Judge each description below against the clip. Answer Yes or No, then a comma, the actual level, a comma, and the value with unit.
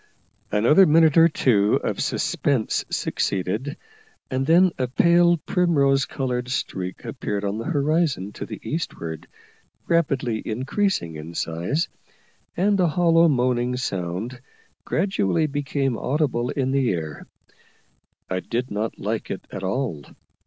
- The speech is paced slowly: Yes, slow, 125 wpm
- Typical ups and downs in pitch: No, wide, 7.3 semitones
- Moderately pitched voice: No, low, 130 Hz